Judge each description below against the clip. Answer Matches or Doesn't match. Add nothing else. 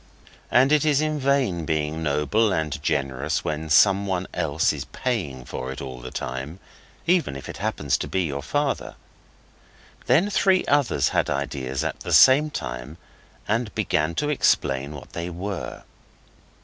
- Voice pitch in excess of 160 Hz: Doesn't match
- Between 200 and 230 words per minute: Doesn't match